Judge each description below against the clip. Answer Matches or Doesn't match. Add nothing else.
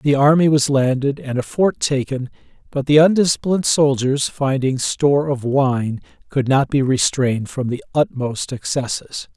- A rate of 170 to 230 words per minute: Doesn't match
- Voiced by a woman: Doesn't match